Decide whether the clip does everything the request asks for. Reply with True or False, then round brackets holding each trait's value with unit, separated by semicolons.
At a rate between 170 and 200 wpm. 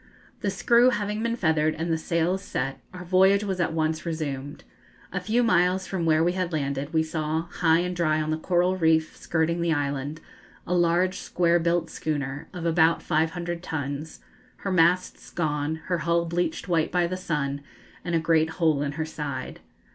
True (185 wpm)